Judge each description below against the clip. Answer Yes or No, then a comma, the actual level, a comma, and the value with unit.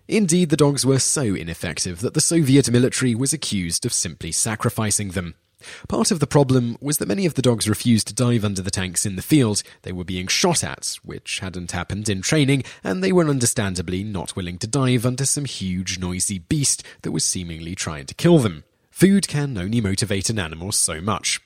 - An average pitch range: No, wide, 6.7 semitones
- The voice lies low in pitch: Yes, low, 110 Hz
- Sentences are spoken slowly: No, fast, 205 wpm